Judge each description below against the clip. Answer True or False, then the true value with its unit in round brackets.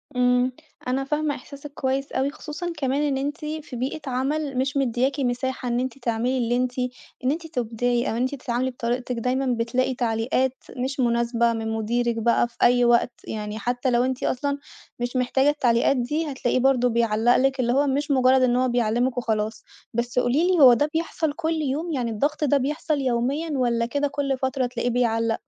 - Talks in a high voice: True (255 Hz)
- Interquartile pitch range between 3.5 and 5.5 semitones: False (2.6 semitones)